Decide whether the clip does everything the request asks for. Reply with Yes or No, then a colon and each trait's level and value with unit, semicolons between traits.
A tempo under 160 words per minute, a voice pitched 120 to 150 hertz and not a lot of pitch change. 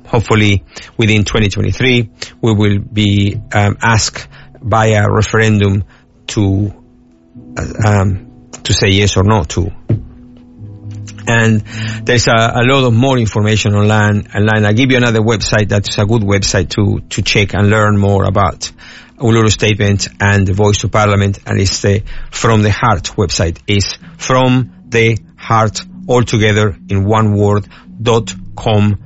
No: average, 145 wpm; low, 105 Hz; narrow, 2.2 semitones